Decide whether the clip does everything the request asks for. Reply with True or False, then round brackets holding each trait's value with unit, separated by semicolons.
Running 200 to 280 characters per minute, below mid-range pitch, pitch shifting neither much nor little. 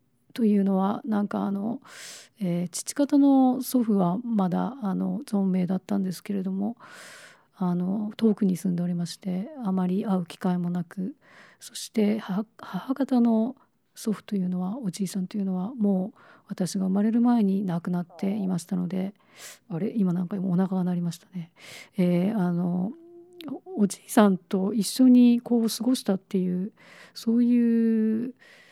False (275 characters per minute; 200 Hz; 3.5 semitones)